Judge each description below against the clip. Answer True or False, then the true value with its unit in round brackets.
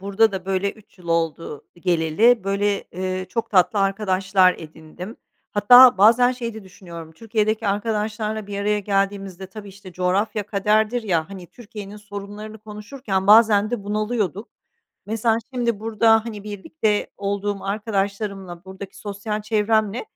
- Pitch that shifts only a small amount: True (2.2 semitones)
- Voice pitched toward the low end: False (205 Hz)